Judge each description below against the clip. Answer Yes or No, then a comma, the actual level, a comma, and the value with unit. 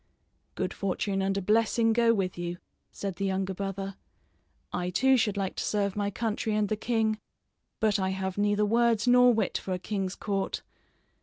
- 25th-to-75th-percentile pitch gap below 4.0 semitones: Yes, narrow, 2.4 semitones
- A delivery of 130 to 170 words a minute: No, average, 180 wpm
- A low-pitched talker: No, high, 205 Hz